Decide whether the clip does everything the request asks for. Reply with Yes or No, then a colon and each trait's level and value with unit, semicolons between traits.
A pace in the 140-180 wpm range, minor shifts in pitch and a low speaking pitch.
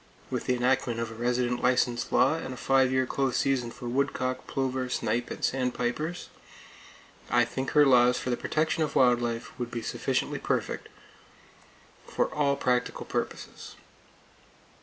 Yes: average, 155 wpm; narrow, 1.7 semitones; low, 125 Hz